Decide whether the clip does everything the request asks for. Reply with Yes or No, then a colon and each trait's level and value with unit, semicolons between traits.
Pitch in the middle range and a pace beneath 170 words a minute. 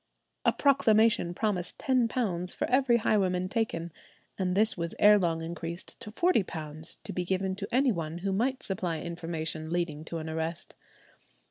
Yes: medium, 180 Hz; average, 155 wpm